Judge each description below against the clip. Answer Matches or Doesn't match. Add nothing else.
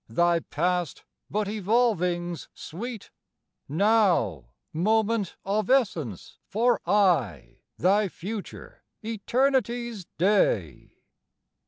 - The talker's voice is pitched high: Matches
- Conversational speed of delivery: Doesn't match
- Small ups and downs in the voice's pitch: Doesn't match